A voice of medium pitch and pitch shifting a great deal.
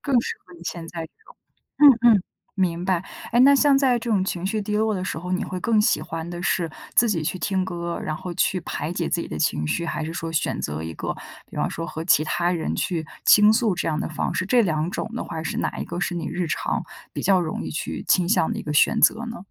No: medium, 180 Hz; average, 4.3 semitones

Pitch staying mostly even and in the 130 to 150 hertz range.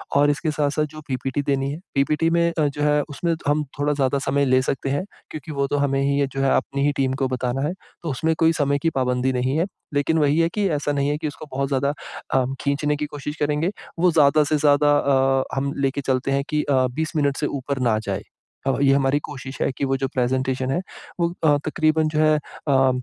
Yes: narrow, 2.0 semitones; medium, 140 Hz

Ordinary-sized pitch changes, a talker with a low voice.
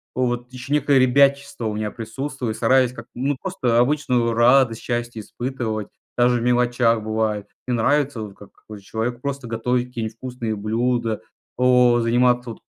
No: narrow, 2.1 semitones; low, 120 Hz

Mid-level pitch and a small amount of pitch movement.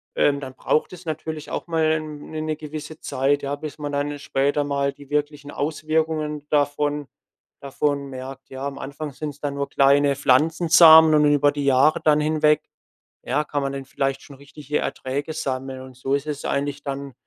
Yes: medium, 145 Hz; narrow, 1.7 semitones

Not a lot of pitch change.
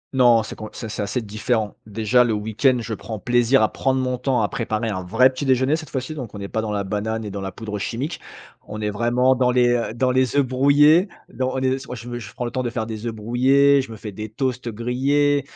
No: average, 3.2 semitones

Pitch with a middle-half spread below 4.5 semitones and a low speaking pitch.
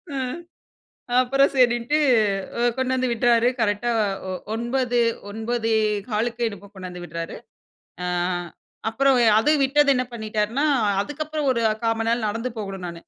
No: average, 3.3 semitones; high, 235 Hz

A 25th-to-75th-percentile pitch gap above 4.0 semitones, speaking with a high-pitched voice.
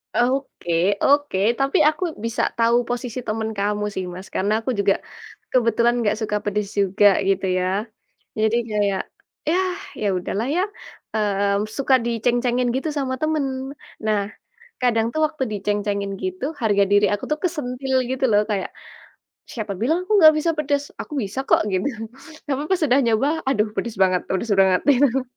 Yes: average, 4.8 semitones; high, 230 Hz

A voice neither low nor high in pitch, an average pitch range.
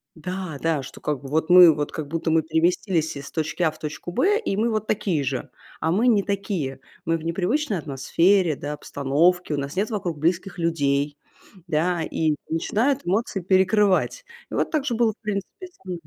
Yes: medium, 170 Hz; average, 4.5 semitones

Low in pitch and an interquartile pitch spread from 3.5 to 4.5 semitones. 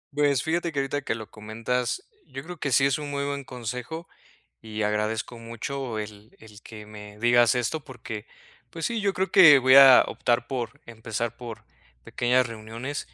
Yes: low, 125 Hz; average, 4.1 semitones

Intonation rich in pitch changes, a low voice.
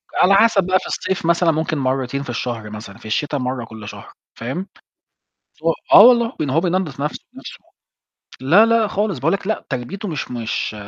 No: wide, 7.4 semitones; medium, 155 Hz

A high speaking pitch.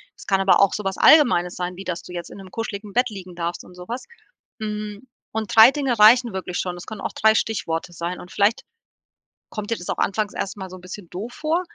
Yes: high, 200 Hz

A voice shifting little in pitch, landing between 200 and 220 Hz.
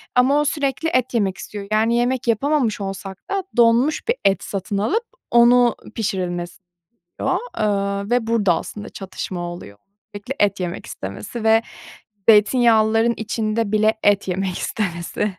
No: average, 3.5 semitones; high, 215 Hz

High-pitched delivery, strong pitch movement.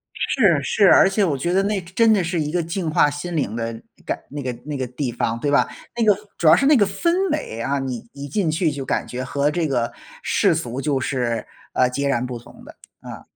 No: medium, 145 Hz; wide, 6.1 semitones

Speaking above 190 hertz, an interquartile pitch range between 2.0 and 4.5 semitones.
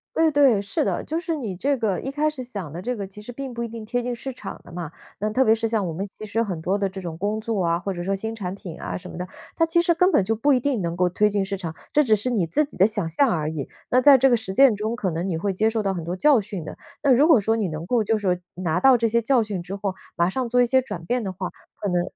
No: high, 210 Hz; average, 5.1 semitones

